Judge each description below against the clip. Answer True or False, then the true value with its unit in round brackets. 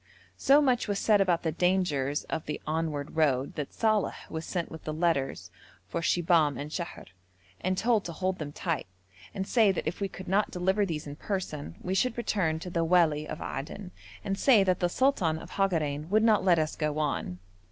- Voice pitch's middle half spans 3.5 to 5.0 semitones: True (4.1 semitones)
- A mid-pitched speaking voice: True (175 Hz)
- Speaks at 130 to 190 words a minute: False (205 wpm)